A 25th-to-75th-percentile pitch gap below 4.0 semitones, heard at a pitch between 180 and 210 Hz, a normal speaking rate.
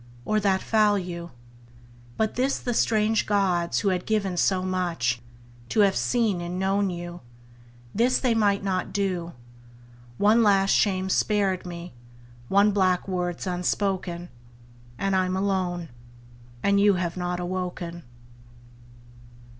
No: narrow, 2.5 semitones; high, 190 Hz; slow, 130 wpm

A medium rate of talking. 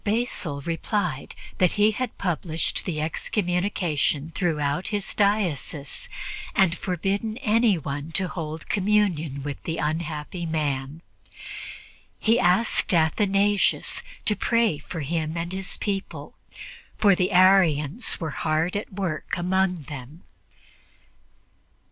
No: slow, 110 wpm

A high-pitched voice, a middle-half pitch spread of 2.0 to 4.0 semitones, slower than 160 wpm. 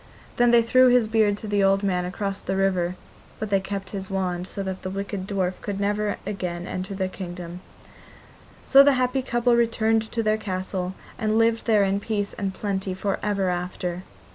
No: high, 200 Hz; narrow, 2.6 semitones; average, 190 wpm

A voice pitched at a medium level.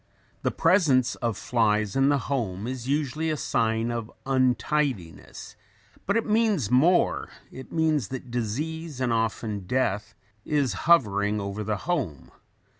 No: low, 125 Hz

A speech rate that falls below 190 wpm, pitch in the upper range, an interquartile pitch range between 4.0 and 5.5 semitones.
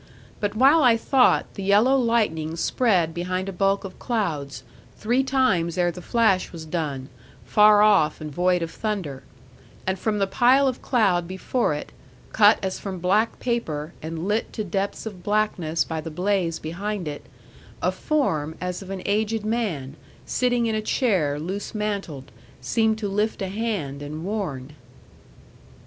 Yes: average, 160 wpm; high, 195 Hz; average, 4.9 semitones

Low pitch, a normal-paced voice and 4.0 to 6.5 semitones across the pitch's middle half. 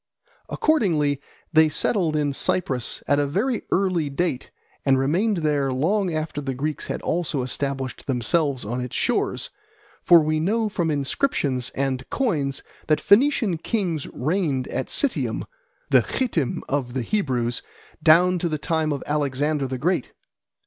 No: medium, 150 Hz; average, 145 wpm; average, 4.8 semitones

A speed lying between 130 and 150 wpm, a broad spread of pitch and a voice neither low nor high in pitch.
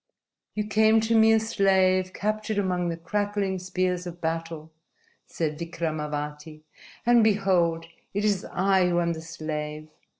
No: average, 140 wpm; average, 3.8 semitones; medium, 180 Hz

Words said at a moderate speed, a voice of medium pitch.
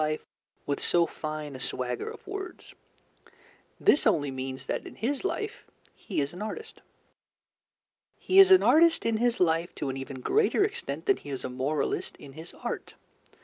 Yes: average, 175 wpm; medium, 165 Hz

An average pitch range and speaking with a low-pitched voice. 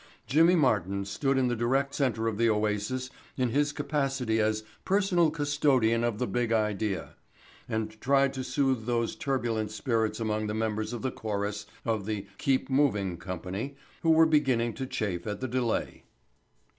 Yes: average, 4.1 semitones; low, 115 Hz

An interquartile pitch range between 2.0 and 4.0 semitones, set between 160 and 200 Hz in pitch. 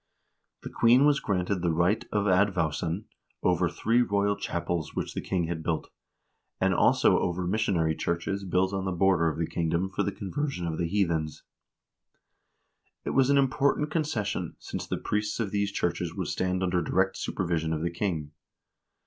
No: average, 3.2 semitones; very low, 95 Hz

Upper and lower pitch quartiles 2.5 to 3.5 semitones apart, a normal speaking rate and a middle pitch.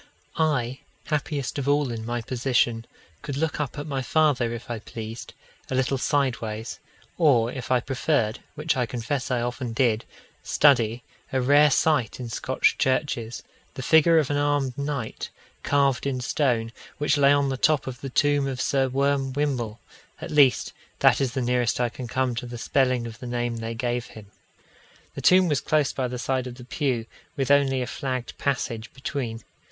No: average, 2.9 semitones; average, 185 wpm; low, 130 Hz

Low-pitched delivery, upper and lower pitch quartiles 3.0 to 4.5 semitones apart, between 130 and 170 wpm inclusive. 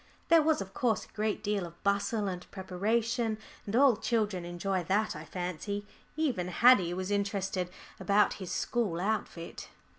No: high, 200 Hz; average, 3.3 semitones; average, 155 wpm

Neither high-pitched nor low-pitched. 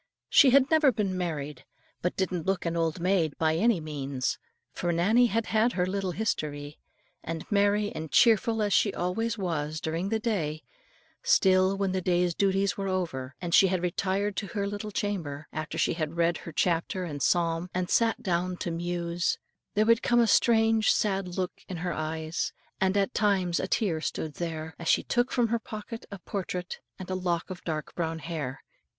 Yes: medium, 180 Hz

